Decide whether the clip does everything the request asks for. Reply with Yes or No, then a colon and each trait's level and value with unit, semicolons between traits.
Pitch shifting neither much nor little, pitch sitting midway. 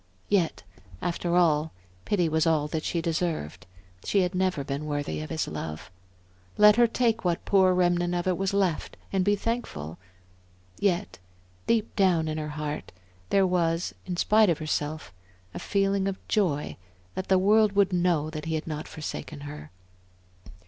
Yes: average, 4.0 semitones; medium, 175 Hz